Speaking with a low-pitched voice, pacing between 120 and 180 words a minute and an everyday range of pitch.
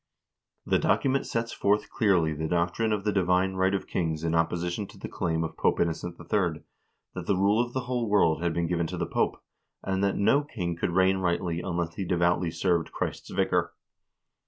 No: very low, 90 Hz; fast, 205 wpm; average, 3.1 semitones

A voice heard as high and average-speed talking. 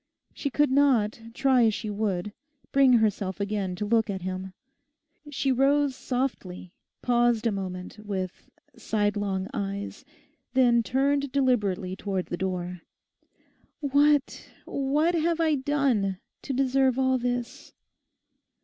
No: high, 235 Hz; slow, 120 wpm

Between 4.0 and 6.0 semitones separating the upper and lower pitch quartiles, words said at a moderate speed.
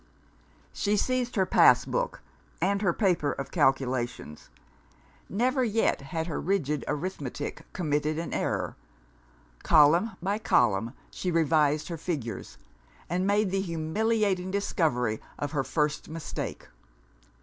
No: wide, 5.4 semitones; slow, 120 wpm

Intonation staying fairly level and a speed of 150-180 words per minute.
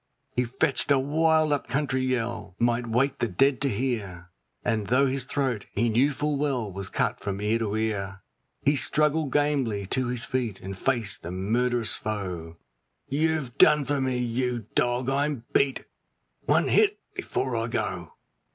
No: average, 4.4 semitones; average, 165 wpm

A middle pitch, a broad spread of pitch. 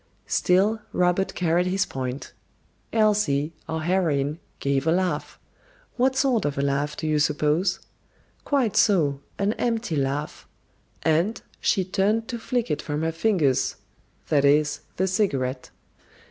Yes: medium, 170 Hz; wide, 5.9 semitones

